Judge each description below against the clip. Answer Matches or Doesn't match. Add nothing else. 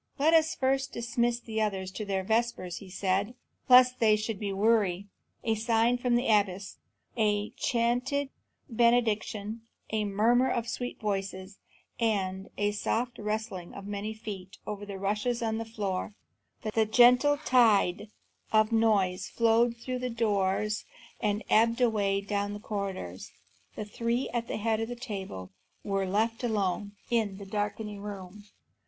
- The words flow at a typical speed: Matches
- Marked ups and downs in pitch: Doesn't match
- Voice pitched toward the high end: Matches